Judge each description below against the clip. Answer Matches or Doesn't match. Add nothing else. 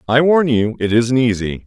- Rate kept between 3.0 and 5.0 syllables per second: Matches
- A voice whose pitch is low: Matches